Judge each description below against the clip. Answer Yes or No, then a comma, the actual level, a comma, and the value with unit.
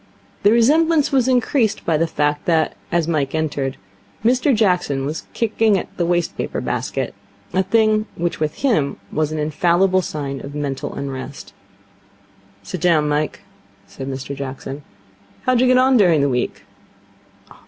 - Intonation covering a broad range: Yes, wide, 7.2 semitones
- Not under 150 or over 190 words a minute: Yes, average, 155 wpm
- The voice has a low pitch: No, medium, 170 Hz